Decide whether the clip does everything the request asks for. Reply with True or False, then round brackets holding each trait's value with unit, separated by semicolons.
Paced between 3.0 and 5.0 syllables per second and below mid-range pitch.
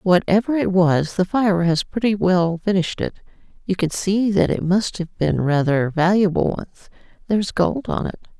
False (4.9 syllables/s; 180 Hz)